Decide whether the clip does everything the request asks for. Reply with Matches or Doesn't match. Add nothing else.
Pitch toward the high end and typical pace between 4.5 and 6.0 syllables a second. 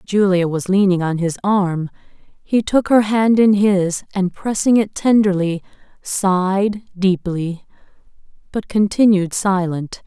Doesn't match